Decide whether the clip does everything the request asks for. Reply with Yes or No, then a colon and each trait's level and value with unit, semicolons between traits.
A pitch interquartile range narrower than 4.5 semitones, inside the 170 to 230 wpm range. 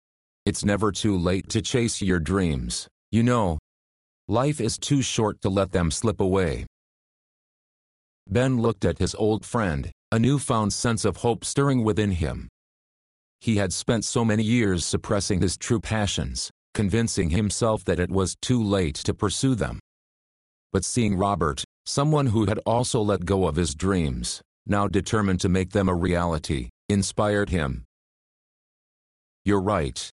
No: average, 4.1 semitones; average, 150 wpm